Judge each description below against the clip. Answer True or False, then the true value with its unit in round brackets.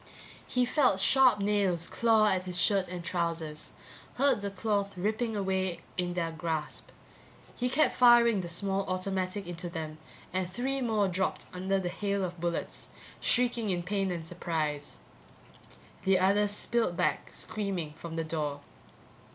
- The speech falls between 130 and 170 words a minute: True (150 wpm)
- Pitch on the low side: False (190 Hz)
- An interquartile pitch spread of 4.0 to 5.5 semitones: False (3.3 semitones)